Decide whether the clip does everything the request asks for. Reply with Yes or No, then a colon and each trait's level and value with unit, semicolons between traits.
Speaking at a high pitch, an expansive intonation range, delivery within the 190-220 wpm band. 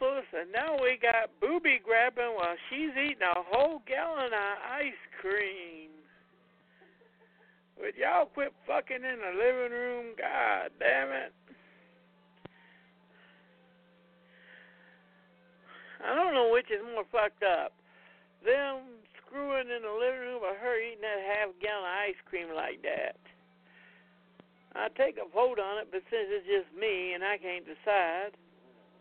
No: high, 225 Hz; wide, 6.9 semitones; slow, 135 wpm